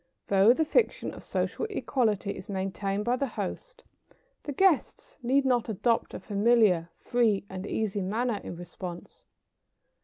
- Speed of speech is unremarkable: Yes, average, 145 wpm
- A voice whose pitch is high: Yes, high, 220 Hz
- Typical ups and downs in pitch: Yes, average, 4.5 semitones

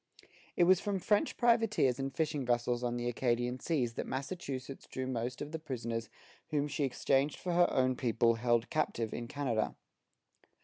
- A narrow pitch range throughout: No, average, 4.2 semitones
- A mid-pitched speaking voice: No, low, 130 Hz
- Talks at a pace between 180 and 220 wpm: No, average, 170 wpm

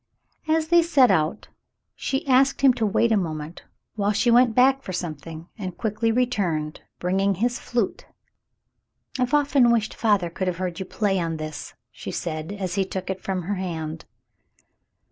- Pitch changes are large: Yes, wide, 5.8 semitones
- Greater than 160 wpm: Yes, average, 170 wpm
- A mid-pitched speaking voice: No, high, 195 Hz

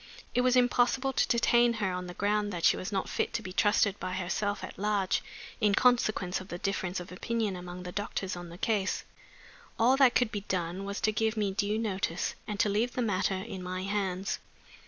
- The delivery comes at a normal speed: No, fast, 215 wpm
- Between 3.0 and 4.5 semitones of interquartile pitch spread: Yes, average, 3.3 semitones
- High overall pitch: Yes, high, 200 Hz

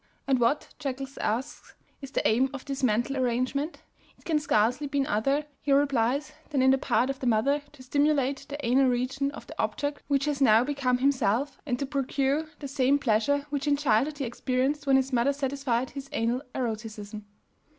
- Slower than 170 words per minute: No, average, 190 wpm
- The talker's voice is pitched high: Yes, very high, 270 Hz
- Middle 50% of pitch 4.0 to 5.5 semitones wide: No, narrow, 2.4 semitones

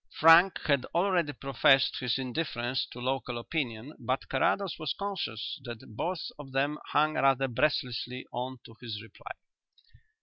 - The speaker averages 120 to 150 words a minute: Yes, average, 140 wpm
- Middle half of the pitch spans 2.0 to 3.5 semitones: No, average, 4.0 semitones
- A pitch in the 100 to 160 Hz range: Yes, low, 135 Hz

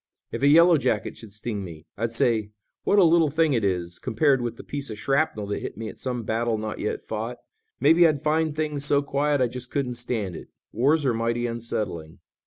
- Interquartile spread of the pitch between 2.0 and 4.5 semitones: No, average, 4.9 semitones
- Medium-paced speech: No, fast, 215 wpm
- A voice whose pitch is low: Yes, low, 120 Hz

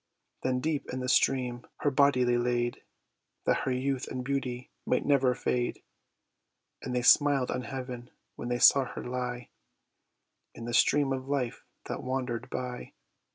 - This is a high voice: No, low, 125 Hz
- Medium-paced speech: Yes, average, 155 wpm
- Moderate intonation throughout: No, narrow, 1.5 semitones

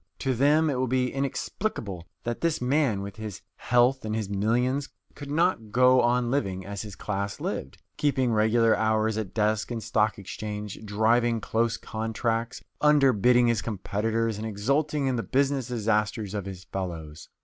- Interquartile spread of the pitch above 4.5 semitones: No, average, 3.5 semitones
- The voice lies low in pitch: Yes, low, 115 Hz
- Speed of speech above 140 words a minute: Yes, average, 160 wpm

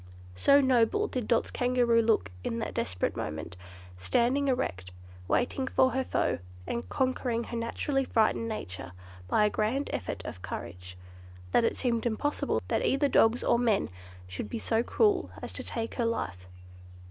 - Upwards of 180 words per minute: No, average, 160 wpm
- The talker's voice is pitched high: Yes, high, 230 Hz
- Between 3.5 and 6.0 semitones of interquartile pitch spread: Yes, average, 4.2 semitones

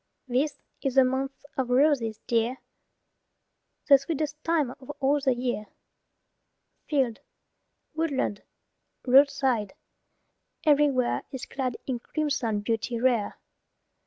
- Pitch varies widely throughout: No, average, 2.9 semitones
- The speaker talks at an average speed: No, slow, 100 wpm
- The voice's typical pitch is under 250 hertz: No, very high, 265 Hz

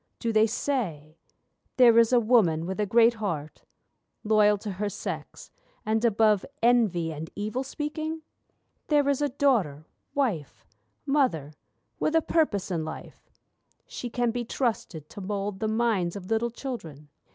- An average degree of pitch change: Yes, average, 4.9 semitones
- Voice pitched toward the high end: Yes, high, 220 Hz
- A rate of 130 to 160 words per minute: Yes, average, 150 wpm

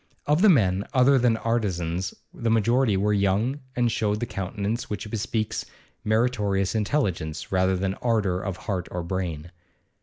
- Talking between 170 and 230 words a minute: No, average, 150 wpm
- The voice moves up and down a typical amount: Yes, average, 3.8 semitones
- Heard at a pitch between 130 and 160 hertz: No, low, 105 Hz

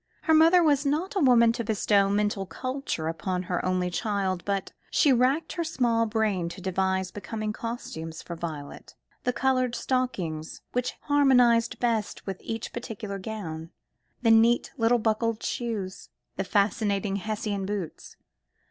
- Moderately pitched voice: No, high, 215 Hz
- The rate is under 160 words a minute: Yes, average, 145 wpm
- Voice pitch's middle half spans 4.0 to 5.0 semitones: Yes, average, 4.5 semitones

